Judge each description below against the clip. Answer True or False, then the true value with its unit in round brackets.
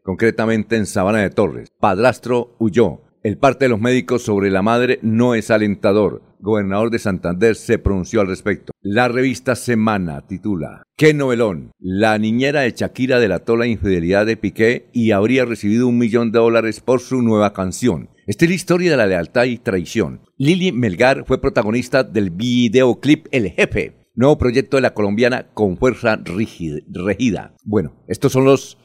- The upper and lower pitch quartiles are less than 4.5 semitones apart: True (3.3 semitones)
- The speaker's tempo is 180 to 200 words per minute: False (165 wpm)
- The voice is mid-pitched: False (115 Hz)